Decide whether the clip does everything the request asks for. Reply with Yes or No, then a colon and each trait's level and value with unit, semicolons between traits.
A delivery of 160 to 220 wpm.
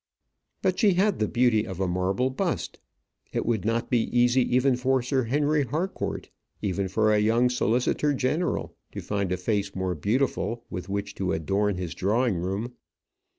Yes: average, 170 wpm